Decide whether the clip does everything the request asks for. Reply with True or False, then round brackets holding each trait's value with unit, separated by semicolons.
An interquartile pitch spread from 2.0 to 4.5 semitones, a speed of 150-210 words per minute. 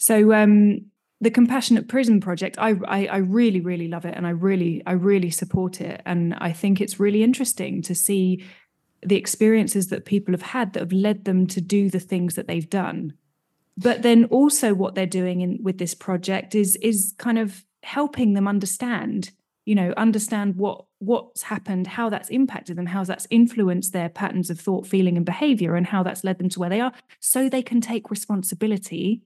True (3.1 semitones; 195 wpm)